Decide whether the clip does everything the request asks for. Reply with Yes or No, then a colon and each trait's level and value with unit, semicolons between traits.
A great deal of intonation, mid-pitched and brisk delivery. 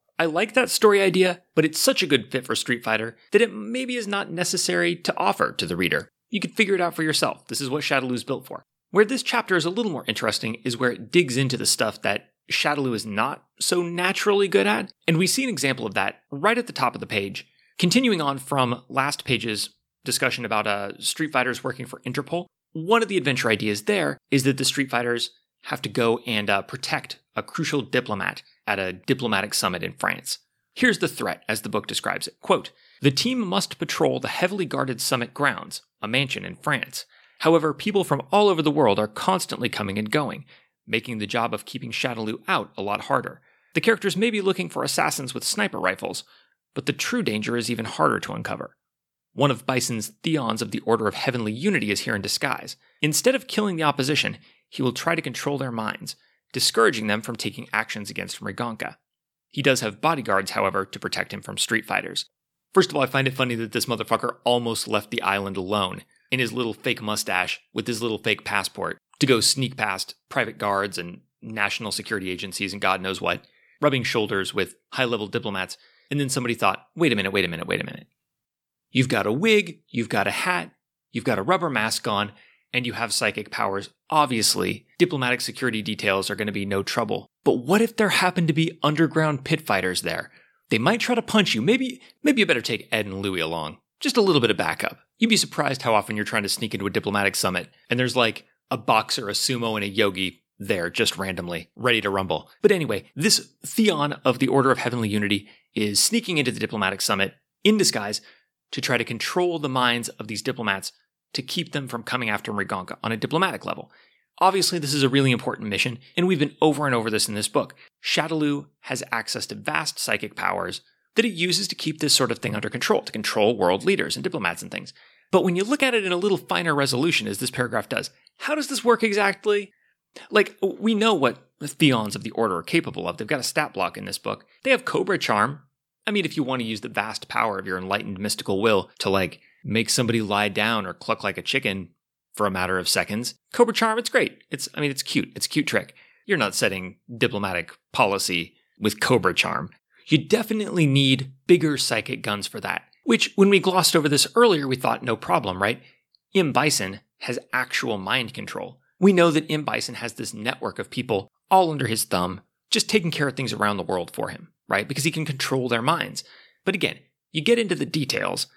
No: wide, 7.9 semitones; low, 130 Hz; fast, 215 wpm